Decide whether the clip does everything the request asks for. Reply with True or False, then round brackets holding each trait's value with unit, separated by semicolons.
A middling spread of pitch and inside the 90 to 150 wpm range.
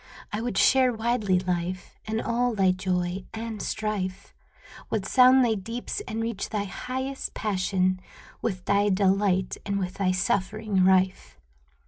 True (3.4 semitones; 140 wpm)